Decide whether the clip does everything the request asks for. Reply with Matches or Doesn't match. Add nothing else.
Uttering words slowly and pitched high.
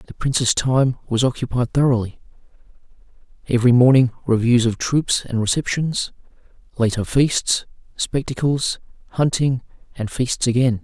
Doesn't match